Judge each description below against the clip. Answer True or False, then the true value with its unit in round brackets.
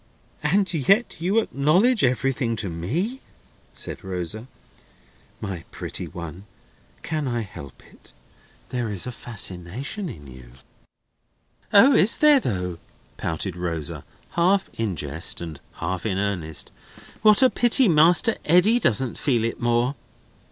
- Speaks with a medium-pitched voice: False (120 Hz)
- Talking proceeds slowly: True (130 wpm)